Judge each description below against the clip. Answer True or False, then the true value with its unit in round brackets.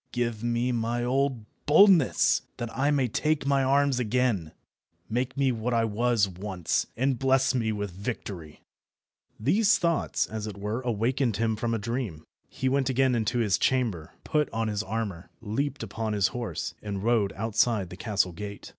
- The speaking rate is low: False (170 wpm)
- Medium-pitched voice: False (115 Hz)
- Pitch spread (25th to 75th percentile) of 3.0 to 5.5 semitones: True (3.9 semitones)